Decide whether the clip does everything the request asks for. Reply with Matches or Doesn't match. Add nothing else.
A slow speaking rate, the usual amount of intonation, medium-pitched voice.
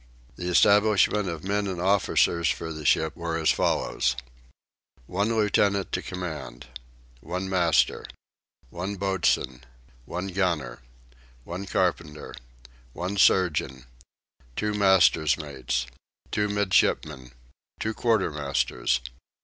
Doesn't match